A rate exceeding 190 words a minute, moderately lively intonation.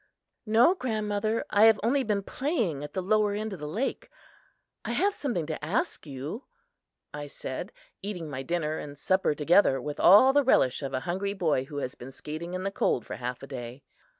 No: average, 200 wpm; wide, 6.8 semitones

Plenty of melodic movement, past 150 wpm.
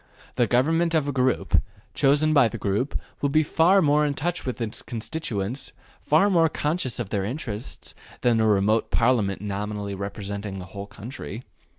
Yes: wide, 6.3 semitones; average, 170 wpm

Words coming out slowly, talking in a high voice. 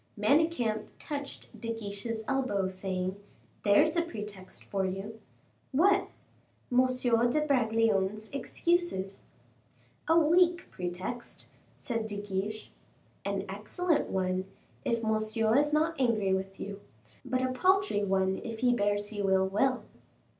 Yes: slow, 125 wpm; high, 220 Hz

